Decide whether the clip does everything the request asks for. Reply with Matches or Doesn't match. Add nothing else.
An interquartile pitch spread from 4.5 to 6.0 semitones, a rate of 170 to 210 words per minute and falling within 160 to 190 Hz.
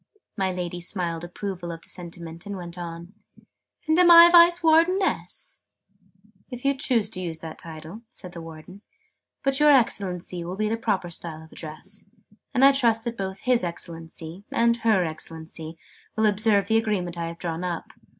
Matches